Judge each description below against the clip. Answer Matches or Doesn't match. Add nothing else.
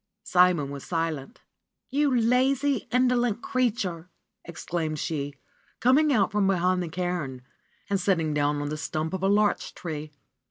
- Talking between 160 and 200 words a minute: Doesn't match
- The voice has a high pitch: Doesn't match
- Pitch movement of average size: Doesn't match